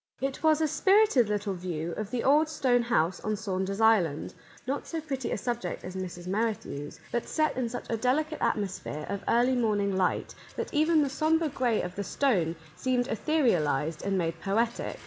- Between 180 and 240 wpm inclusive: Yes, average, 185 wpm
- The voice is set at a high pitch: Yes, high, 225 Hz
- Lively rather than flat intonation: Yes, wide, 6.4 semitones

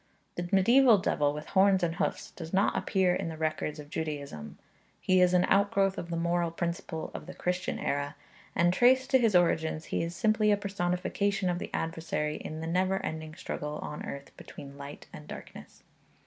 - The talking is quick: No, average, 190 wpm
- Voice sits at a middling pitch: Yes, medium, 175 Hz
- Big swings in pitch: No, average, 3.6 semitones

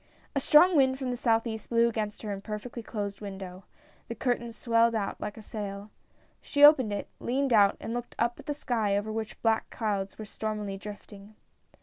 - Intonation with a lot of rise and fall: No, average, 2.7 semitones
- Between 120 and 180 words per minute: No, average, 190 wpm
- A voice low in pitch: No, high, 220 Hz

